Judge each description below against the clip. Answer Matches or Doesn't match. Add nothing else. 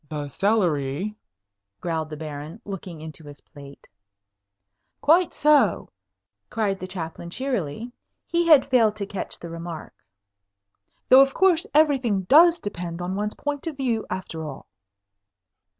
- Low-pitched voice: Doesn't match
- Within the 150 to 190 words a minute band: Doesn't match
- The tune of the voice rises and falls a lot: Matches